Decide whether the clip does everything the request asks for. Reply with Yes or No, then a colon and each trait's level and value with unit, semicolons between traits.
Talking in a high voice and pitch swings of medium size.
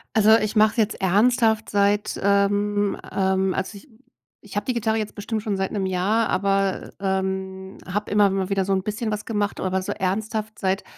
No: high, 205 Hz; narrow, 1.9 semitones